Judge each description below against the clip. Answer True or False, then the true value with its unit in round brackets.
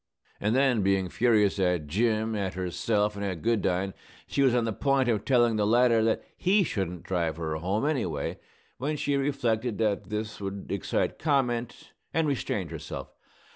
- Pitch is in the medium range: False (110 Hz)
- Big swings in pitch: False (4.3 semitones)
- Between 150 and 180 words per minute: True (170 wpm)